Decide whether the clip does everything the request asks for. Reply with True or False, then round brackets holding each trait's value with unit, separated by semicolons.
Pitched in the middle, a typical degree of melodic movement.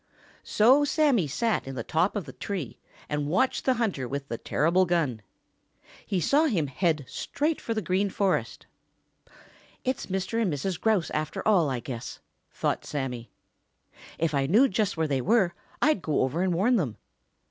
False (180 Hz; 7.2 semitones)